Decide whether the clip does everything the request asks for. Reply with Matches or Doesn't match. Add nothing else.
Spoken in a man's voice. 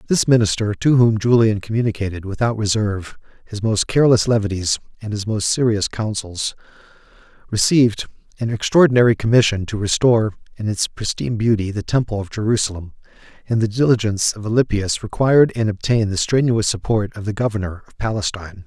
Matches